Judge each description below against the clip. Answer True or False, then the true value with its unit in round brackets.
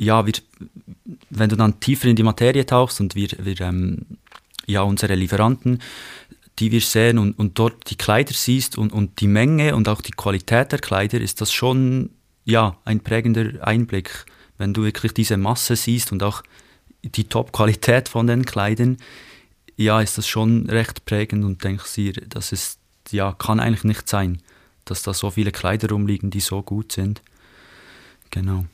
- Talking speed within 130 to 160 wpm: False (175 wpm)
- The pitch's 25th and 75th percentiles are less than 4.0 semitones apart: True (2.7 semitones)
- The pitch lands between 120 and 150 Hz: False (110 Hz)